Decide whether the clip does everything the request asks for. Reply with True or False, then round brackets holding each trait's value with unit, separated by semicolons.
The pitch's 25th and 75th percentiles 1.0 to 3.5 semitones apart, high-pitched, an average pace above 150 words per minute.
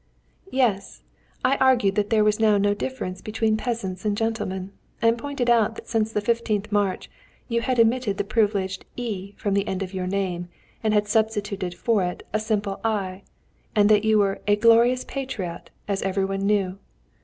True (2.7 semitones; 210 Hz; 180 wpm)